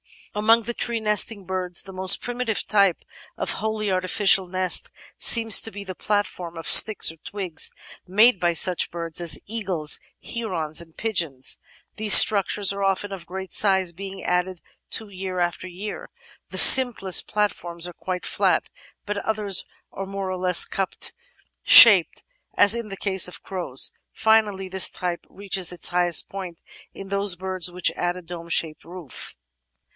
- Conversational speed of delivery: Yes, average, 160 wpm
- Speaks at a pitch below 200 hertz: Yes, high, 190 Hz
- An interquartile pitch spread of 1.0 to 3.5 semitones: Yes, narrow, 2.6 semitones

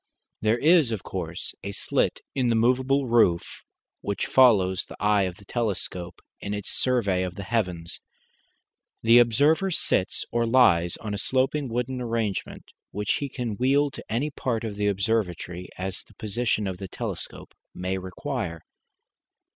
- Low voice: Yes, low, 110 Hz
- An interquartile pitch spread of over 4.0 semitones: Yes, average, 4.8 semitones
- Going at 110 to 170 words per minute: Yes, average, 155 wpm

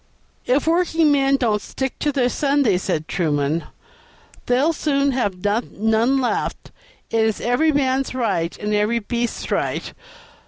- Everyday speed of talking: No, slow, 130 wpm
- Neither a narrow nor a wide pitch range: Yes, average, 4.8 semitones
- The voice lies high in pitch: Yes, high, 245 Hz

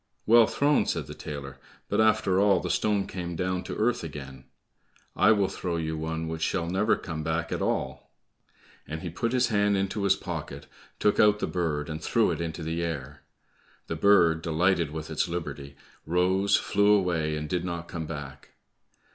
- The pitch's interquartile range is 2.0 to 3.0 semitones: No, average, 3.7 semitones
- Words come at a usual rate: Yes, average, 185 wpm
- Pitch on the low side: Yes, very low, 85 Hz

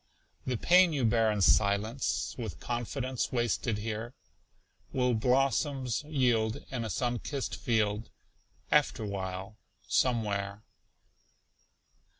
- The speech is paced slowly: Yes, slow, 100 wpm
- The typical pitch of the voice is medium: No, low, 115 Hz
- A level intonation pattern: No, average, 3.3 semitones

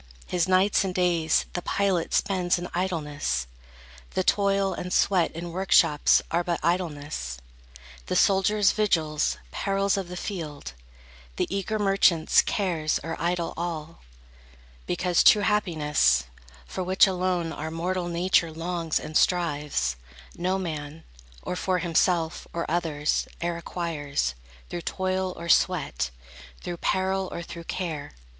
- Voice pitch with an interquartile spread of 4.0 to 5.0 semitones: No, average, 2.8 semitones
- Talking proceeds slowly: Yes, slow, 130 wpm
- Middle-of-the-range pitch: Yes, medium, 175 Hz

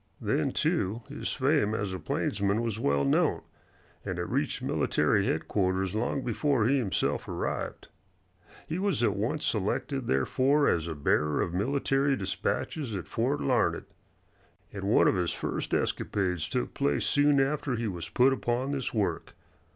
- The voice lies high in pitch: No, low, 115 Hz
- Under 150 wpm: No, average, 155 wpm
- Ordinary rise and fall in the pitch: No, wide, 6.3 semitones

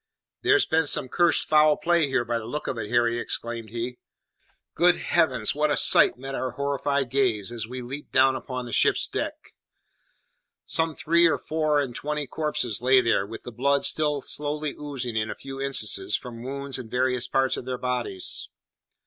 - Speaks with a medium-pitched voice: No, low, 130 Hz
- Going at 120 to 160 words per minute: No, average, 185 wpm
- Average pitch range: Yes, average, 3.6 semitones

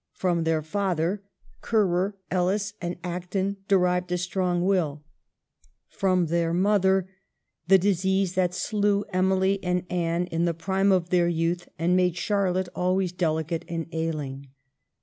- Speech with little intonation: Yes, narrow, 2.0 semitones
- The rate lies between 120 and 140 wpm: Yes, slow, 135 wpm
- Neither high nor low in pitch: Yes, medium, 180 Hz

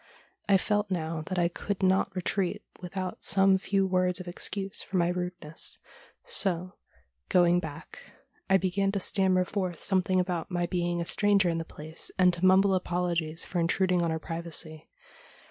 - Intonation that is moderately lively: No, narrow, 1.9 semitones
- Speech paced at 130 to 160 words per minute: No, average, 170 wpm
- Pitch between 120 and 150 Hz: No, medium, 180 Hz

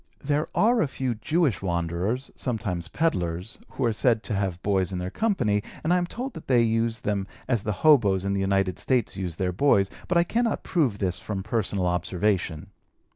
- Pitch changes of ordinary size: No, wide, 6.3 semitones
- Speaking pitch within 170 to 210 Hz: No, low, 105 Hz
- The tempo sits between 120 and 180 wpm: No, average, 195 wpm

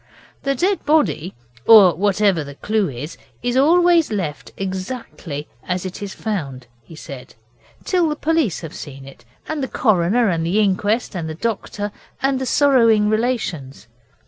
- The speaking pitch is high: Yes, high, 205 Hz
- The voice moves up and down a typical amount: No, wide, 7.6 semitones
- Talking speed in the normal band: Yes, average, 155 wpm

